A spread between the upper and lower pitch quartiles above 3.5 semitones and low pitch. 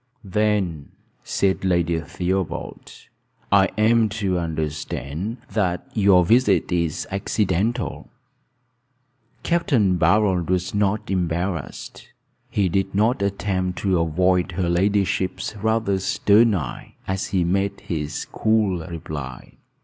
No: average, 3.0 semitones; very low, 95 Hz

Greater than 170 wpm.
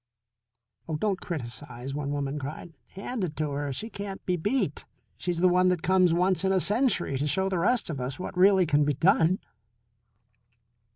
Yes: average, 185 wpm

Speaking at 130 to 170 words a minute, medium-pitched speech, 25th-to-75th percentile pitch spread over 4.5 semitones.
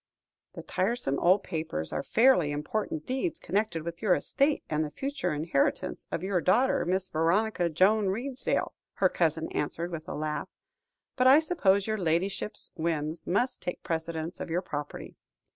Yes: average, 160 wpm; medium, 180 Hz; average, 5.2 semitones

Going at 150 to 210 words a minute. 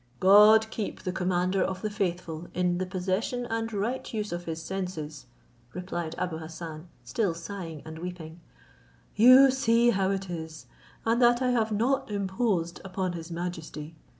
Yes: average, 155 wpm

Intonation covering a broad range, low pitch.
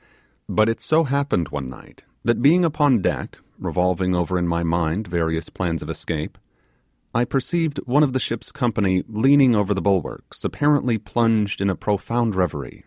Yes: wide, 6.5 semitones; low, 105 Hz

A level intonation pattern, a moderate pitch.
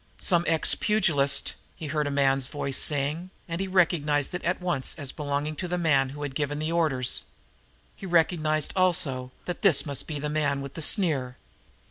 No: average, 3.6 semitones; medium, 150 Hz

